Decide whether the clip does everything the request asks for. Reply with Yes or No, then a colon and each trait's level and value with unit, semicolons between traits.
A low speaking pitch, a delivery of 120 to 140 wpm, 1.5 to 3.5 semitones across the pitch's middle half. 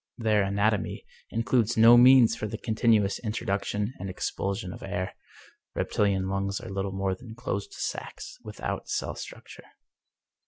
Yes: low, 105 Hz; slow, 135 wpm; average, 2.8 semitones